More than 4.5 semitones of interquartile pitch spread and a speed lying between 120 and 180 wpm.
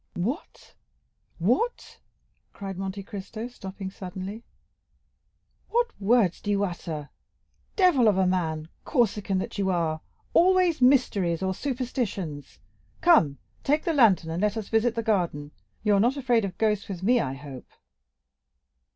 Yes: average, 5.1 semitones; slow, 135 wpm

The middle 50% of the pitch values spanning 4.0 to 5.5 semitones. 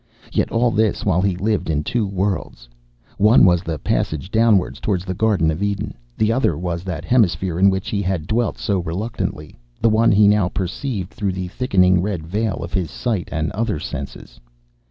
No: average, 3.5 semitones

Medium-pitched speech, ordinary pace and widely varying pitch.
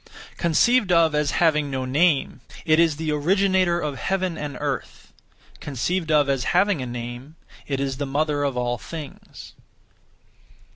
No: medium, 150 Hz; average, 150 wpm; average, 3.9 semitones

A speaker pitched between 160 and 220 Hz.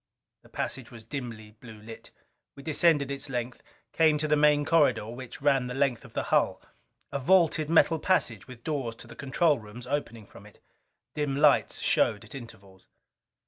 No: low, 135 Hz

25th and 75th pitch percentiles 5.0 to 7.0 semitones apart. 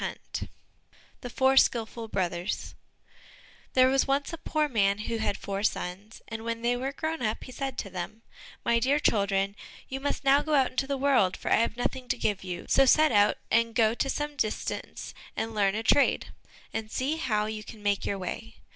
No: average, 4.4 semitones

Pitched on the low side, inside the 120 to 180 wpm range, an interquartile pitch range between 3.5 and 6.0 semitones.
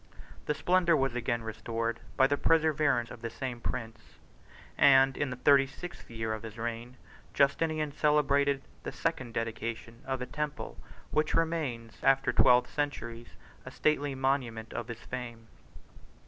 Yes: low, 130 Hz; average, 150 wpm; average, 3.8 semitones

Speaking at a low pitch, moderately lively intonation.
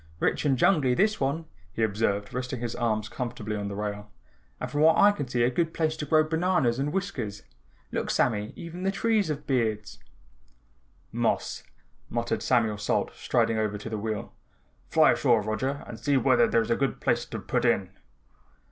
No: low, 125 Hz; wide, 5.9 semitones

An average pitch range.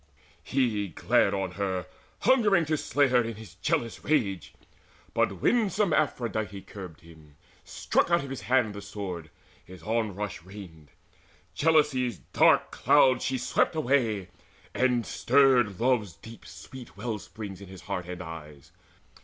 No: wide, 5.8 semitones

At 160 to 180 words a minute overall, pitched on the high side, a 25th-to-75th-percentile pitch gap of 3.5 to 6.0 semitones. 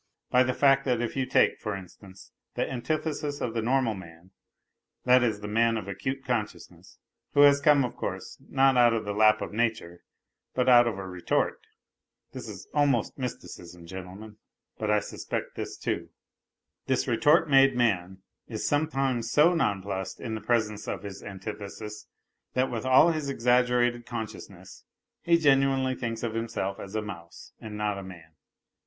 No: average, 165 wpm; low, 115 Hz; average, 4.4 semitones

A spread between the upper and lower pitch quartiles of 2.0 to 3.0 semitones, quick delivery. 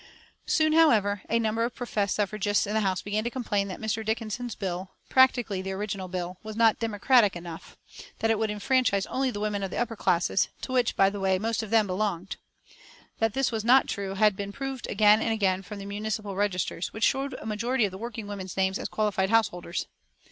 Yes: average, 2.7 semitones; fast, 210 wpm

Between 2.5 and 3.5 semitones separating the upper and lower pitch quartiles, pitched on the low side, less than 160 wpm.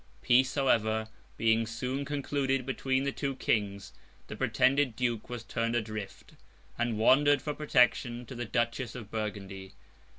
Yes: average, 3.2 semitones; low, 120 Hz; average, 140 wpm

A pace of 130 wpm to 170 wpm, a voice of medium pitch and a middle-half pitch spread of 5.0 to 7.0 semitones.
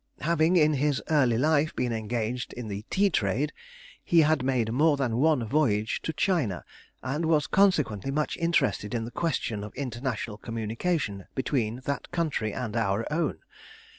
No: average, 160 wpm; low, 130 Hz; wide, 5.5 semitones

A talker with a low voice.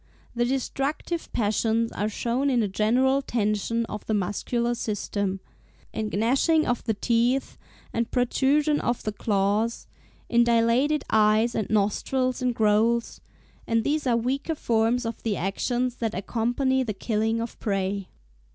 No: high, 230 Hz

